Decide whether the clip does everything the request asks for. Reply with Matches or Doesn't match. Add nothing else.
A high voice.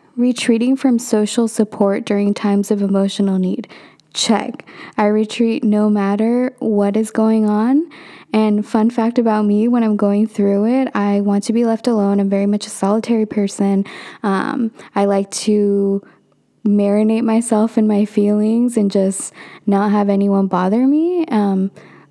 Matches